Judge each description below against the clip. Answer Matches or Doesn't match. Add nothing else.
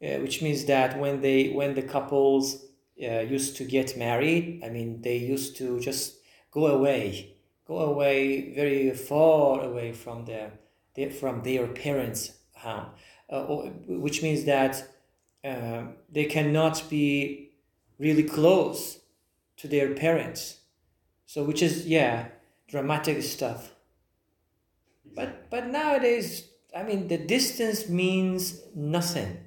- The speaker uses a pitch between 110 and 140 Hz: Matches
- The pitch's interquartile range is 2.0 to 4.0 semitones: Doesn't match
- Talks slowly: Matches